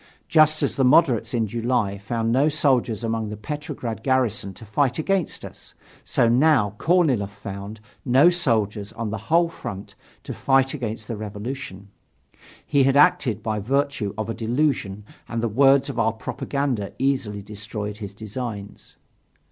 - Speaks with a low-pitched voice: Yes, low, 115 Hz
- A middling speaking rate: Yes, average, 155 wpm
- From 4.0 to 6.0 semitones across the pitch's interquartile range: Yes, average, 4.7 semitones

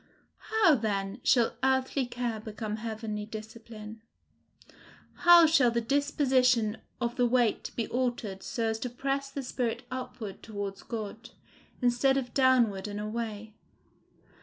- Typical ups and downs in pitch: Yes, average, 3.1 semitones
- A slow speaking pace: Yes, slow, 130 wpm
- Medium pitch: No, high, 235 Hz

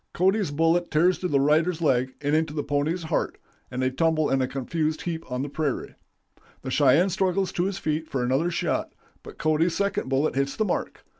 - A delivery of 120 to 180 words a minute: No, average, 200 wpm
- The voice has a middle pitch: Yes, medium, 155 Hz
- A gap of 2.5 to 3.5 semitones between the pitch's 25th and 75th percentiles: No, average, 3.9 semitones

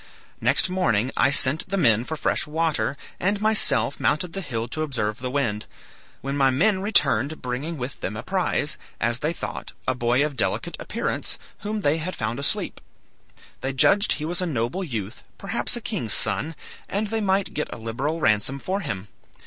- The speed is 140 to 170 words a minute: No, average, 185 wpm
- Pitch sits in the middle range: Yes, medium, 145 Hz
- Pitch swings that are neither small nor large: No, wide, 7.0 semitones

